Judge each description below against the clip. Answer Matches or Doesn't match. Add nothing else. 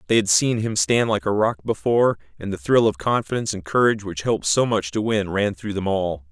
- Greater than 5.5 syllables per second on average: Matches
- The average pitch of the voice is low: Matches